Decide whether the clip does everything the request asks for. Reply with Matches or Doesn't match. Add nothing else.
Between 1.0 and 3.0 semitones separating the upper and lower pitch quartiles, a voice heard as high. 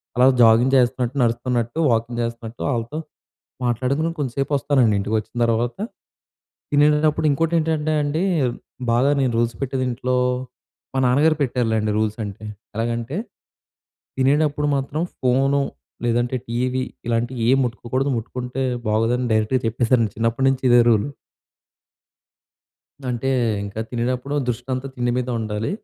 Doesn't match